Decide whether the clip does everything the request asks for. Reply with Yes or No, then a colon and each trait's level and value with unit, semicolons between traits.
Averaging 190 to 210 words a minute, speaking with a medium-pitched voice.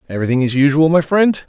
Yes: fast, 205 wpm; medium, 150 Hz